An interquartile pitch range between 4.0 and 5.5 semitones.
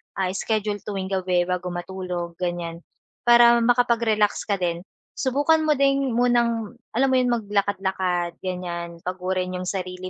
Yes: average, 4.6 semitones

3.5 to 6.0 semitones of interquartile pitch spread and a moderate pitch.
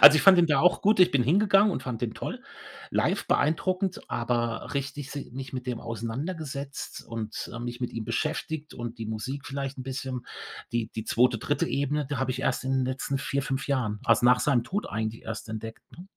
No: average, 3.8 semitones; low, 130 Hz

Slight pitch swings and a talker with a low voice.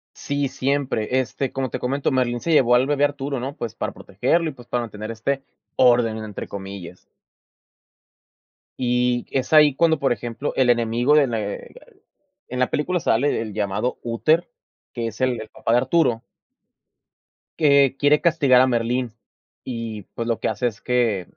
No: average, 3.4 semitones; low, 125 Hz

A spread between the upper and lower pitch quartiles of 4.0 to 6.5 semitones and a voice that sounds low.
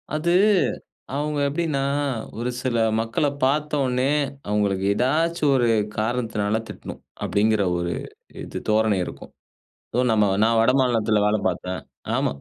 Yes: average, 4.6 semitones; low, 120 Hz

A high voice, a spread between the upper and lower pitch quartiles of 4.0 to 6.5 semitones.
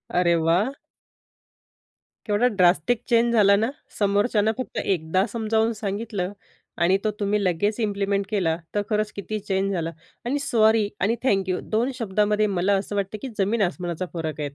No: high, 205 Hz; average, 2.7 semitones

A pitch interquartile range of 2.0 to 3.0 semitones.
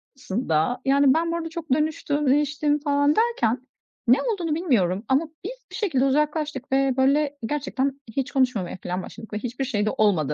No: average, 3.5 semitones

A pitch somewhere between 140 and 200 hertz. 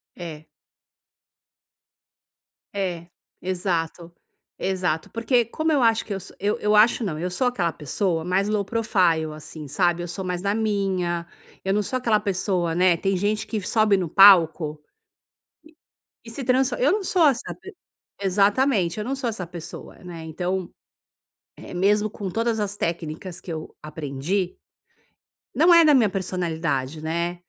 Yes: high, 190 Hz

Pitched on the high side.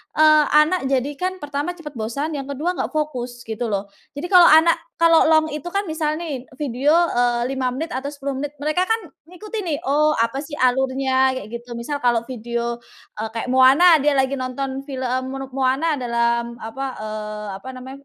Yes: very high, 270 Hz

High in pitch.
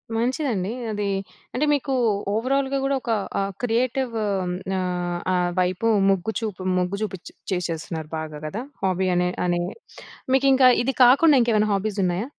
Yes: high, 210 Hz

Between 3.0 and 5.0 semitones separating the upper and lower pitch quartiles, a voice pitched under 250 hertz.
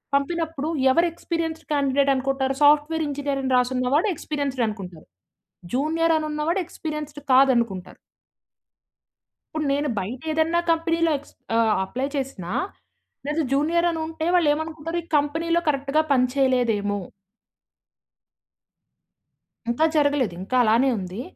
No: average, 3.7 semitones; very high, 285 Hz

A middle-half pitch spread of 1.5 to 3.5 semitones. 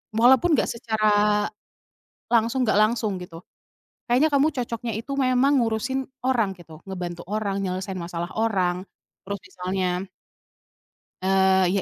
No: average, 4.2 semitones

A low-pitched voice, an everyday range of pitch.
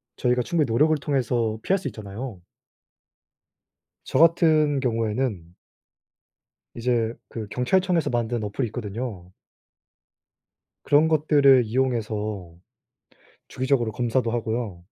Yes: low, 120 Hz; average, 4.0 semitones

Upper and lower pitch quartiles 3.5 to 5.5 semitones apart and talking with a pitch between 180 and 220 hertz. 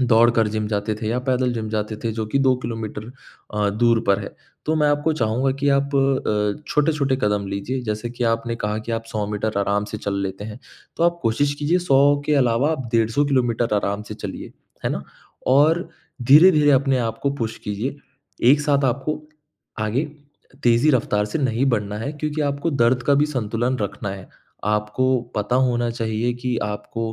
No: average, 4.5 semitones; low, 120 Hz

